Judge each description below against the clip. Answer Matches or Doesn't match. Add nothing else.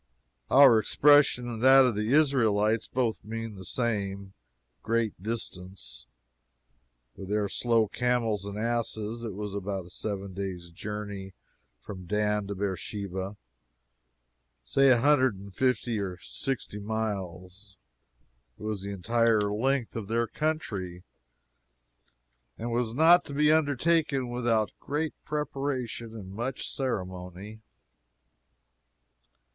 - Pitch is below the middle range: Matches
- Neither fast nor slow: Doesn't match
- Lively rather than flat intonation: Doesn't match